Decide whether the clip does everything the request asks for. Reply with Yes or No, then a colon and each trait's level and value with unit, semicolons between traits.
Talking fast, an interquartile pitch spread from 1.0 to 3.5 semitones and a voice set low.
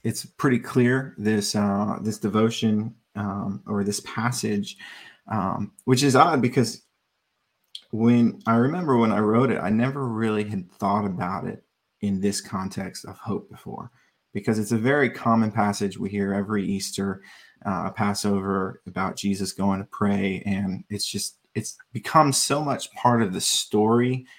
No: average, 155 wpm; average, 3.2 semitones; low, 105 Hz